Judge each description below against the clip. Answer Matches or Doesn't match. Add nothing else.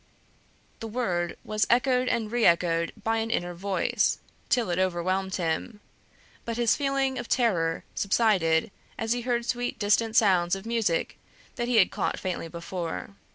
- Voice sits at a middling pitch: Doesn't match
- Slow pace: Doesn't match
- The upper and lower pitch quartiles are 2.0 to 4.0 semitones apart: Doesn't match